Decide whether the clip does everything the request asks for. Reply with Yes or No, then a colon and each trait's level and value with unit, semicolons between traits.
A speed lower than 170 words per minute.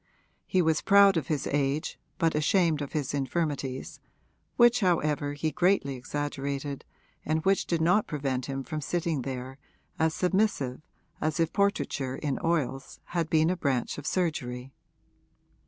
Yes: average, 145 wpm